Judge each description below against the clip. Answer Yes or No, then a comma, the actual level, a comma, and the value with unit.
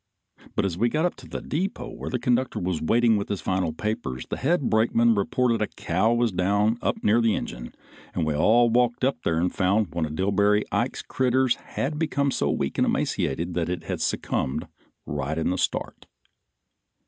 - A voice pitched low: Yes, low, 105 Hz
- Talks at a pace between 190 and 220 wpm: Yes, average, 200 wpm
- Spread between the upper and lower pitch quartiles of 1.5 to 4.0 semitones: No, wide, 5.5 semitones